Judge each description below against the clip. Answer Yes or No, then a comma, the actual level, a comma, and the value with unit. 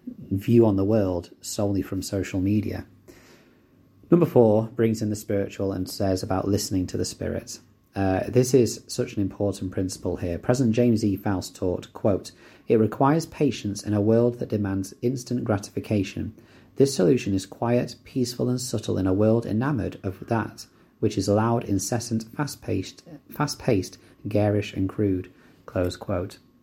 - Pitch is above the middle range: No, low, 105 Hz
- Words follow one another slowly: No, average, 160 wpm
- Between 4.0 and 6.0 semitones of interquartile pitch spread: No, average, 3.6 semitones